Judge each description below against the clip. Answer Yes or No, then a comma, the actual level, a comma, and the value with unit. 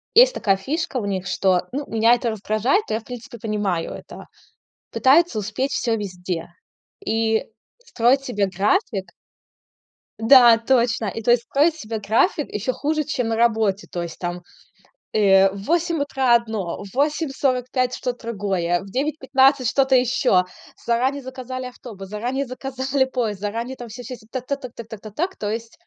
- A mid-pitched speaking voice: No, high, 235 Hz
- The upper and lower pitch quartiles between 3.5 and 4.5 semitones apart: Yes, average, 4.2 semitones